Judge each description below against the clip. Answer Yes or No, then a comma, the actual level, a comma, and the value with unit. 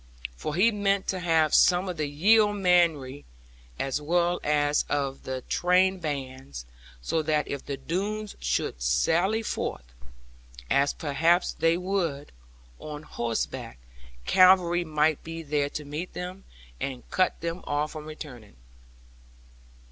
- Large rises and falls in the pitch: No, average, 4.0 semitones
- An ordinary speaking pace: No, slow, 130 wpm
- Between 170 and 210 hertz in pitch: No, medium, 155 Hz